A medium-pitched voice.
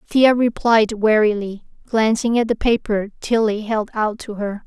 No: high, 220 Hz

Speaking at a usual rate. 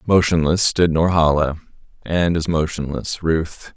No: slow, 110 wpm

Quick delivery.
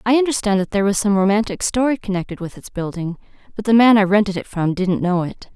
Yes: fast, 240 wpm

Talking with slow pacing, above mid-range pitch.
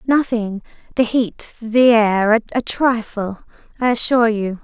Yes: slow, 130 wpm; high, 230 Hz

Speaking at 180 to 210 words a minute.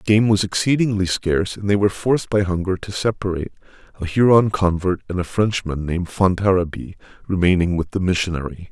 No: average, 165 wpm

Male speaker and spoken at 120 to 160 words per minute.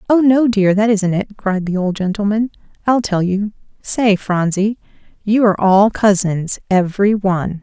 No: female; average, 155 wpm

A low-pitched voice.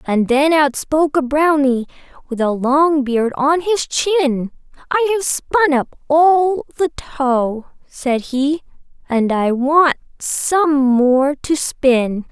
No: very high, 285 Hz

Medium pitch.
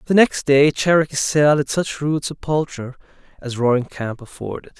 Yes: medium, 145 Hz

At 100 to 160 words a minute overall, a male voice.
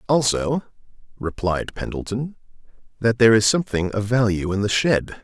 Yes: average, 140 wpm; male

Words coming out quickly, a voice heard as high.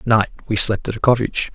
No: fast, 270 wpm; low, 110 Hz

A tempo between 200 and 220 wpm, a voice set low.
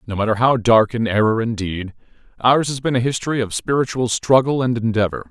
Yes: fast, 205 wpm; low, 120 Hz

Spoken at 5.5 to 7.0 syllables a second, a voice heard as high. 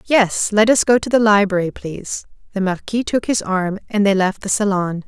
No: 5.0 syllables/s; high, 205 Hz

